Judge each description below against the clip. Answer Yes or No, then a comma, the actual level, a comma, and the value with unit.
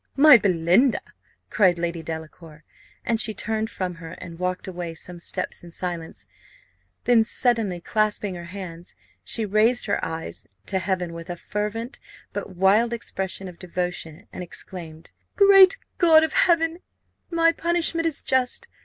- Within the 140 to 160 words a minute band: Yes, average, 145 wpm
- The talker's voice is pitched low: No, high, 190 Hz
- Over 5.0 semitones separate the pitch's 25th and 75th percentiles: Yes, wide, 5.6 semitones